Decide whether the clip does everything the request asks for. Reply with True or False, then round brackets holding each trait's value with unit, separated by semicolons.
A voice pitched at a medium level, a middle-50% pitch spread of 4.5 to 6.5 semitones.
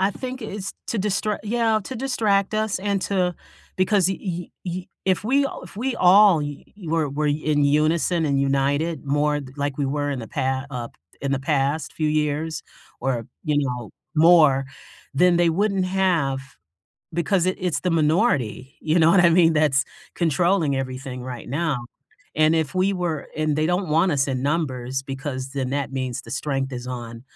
True (155 Hz; 5.0 semitones)